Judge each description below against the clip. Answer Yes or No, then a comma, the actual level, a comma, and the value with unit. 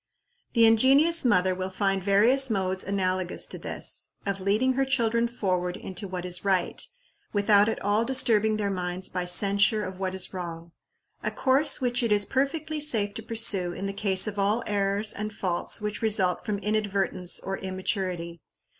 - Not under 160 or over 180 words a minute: Yes, average, 170 wpm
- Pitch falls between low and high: No, high, 200 Hz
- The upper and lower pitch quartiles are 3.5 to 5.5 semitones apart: No, average, 3.1 semitones